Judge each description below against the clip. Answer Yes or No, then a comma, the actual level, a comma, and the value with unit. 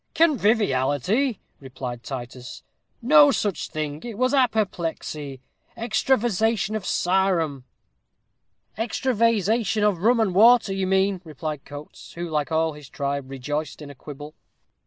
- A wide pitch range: Yes, wide, 7.3 semitones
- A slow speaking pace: Yes, slow, 130 wpm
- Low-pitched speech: No, medium, 185 Hz